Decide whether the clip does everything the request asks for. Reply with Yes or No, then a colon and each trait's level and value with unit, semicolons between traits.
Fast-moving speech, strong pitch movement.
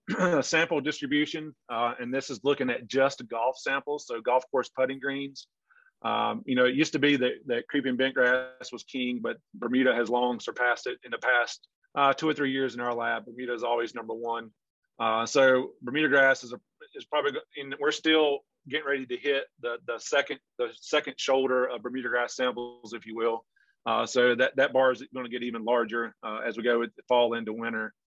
No: fast, 215 wpm; average, 2.9 semitones